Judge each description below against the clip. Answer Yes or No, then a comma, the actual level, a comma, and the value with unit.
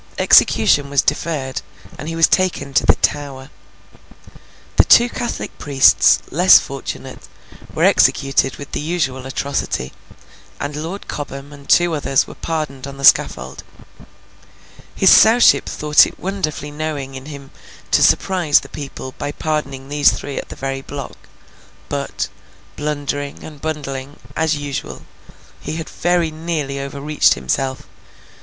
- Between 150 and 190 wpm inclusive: No, slow, 135 wpm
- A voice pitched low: No, medium, 145 Hz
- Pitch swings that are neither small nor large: No, narrow, 2.3 semitones